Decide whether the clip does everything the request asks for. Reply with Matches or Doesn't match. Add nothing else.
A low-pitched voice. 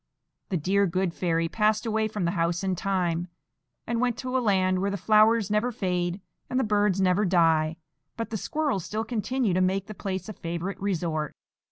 Doesn't match